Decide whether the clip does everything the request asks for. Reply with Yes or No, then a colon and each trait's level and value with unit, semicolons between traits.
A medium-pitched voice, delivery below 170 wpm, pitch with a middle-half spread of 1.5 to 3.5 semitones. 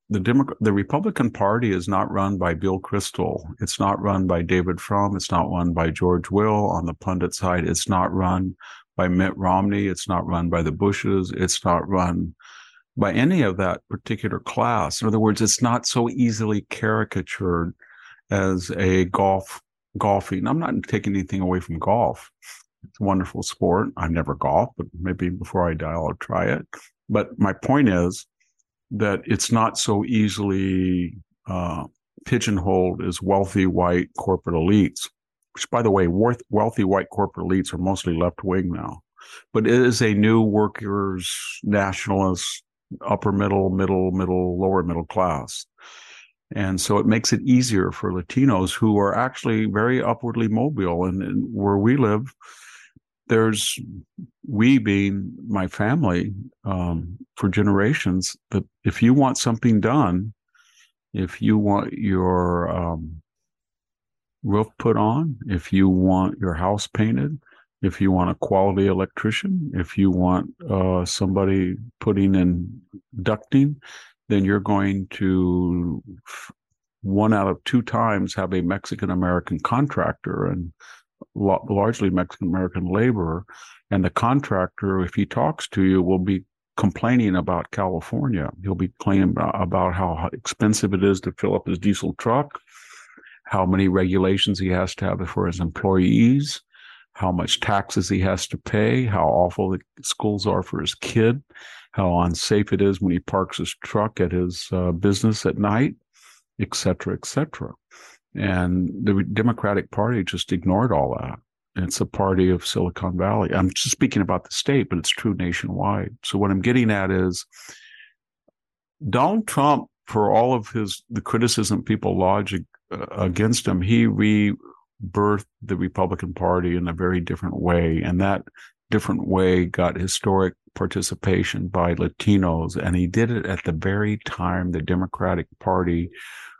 No: very low, 95 Hz; average, 155 wpm; average, 2.8 semitones